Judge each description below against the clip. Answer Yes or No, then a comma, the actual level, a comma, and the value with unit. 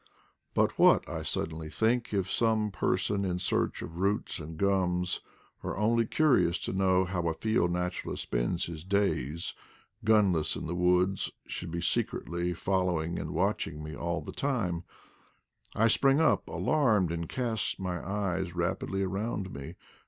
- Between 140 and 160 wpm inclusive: Yes, average, 150 wpm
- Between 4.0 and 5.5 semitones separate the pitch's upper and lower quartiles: No, average, 3.3 semitones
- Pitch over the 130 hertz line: No, very low, 90 Hz